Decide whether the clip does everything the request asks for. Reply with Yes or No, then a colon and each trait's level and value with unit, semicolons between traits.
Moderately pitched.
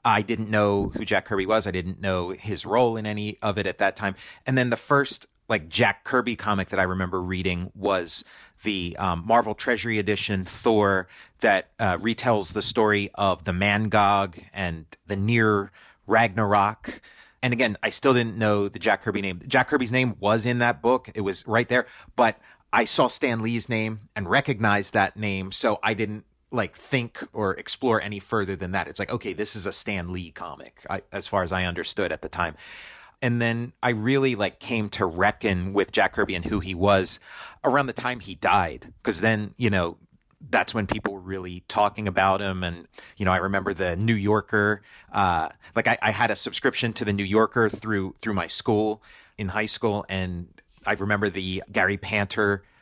No: low, 105 Hz